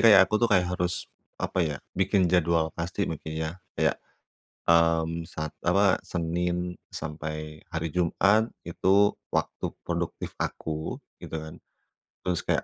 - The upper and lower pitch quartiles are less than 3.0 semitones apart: Yes, narrow, 2.4 semitones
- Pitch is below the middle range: Yes, very low, 85 Hz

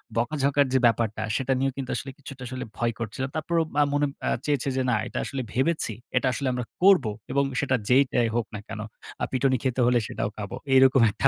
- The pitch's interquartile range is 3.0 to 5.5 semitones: No, narrow, 2.6 semitones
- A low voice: Yes, low, 130 Hz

